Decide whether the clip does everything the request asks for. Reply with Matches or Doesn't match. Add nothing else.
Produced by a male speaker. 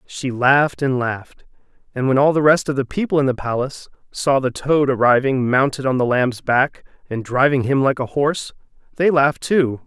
Matches